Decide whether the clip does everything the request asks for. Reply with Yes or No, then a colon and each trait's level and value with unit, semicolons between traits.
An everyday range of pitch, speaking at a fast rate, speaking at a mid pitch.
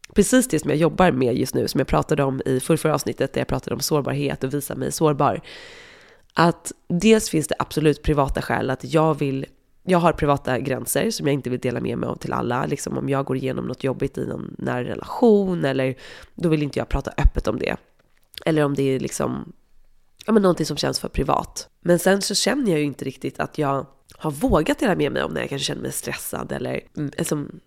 Yes: average, 4.2 semitones; fast, 225 wpm; medium, 150 Hz